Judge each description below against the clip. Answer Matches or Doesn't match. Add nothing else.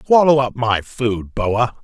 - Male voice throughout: Matches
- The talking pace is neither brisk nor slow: Matches